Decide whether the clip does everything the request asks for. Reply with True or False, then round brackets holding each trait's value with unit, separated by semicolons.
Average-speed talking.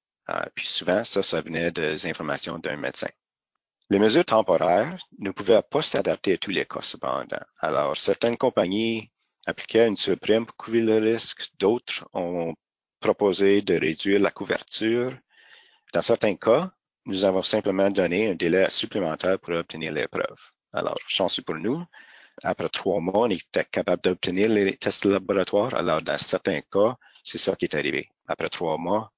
True (165 wpm)